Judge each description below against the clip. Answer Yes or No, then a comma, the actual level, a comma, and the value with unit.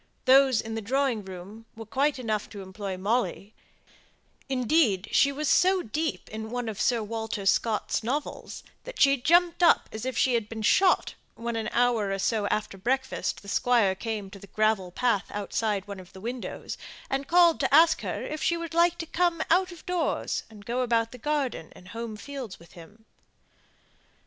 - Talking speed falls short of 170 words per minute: No, average, 185 wpm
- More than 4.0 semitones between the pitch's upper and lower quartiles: Yes, average, 5.0 semitones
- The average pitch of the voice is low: No, high, 230 Hz